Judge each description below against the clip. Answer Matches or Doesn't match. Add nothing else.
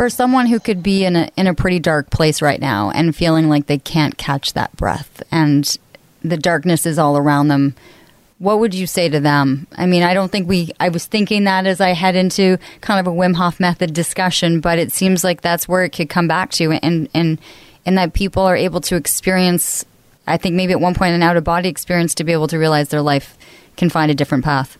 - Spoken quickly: Matches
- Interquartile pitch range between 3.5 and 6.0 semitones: Doesn't match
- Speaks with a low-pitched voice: Doesn't match